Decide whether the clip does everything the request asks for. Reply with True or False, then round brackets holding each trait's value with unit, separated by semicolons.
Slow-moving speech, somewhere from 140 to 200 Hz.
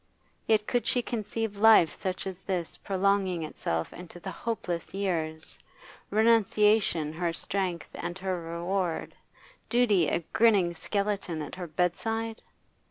True (125 wpm; 190 Hz)